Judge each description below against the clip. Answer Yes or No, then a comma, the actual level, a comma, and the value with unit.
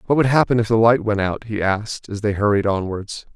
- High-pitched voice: No, low, 105 Hz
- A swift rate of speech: Yes, fast, 250 wpm